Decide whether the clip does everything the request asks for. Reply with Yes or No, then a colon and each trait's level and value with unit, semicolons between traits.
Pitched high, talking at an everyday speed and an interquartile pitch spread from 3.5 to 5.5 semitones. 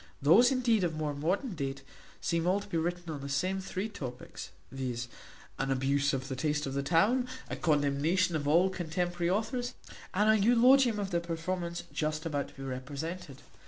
No: medium, 165 Hz; average, 185 wpm; average, 5.1 semitones